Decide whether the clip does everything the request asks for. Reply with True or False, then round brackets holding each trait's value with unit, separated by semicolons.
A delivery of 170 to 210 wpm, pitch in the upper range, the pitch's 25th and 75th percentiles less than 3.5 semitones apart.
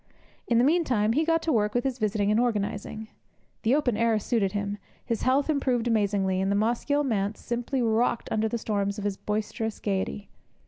True (190 wpm; 220 Hz; 3.1 semitones)